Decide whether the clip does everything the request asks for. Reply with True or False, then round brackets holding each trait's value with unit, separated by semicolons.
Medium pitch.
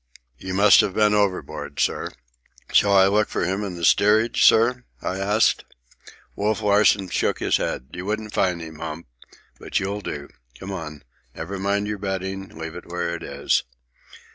False (95 Hz)